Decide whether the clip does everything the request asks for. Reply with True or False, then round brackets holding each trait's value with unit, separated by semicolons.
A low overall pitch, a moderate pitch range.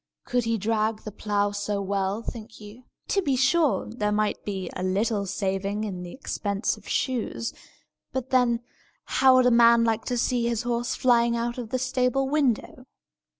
False (230 Hz; 3.2 semitones)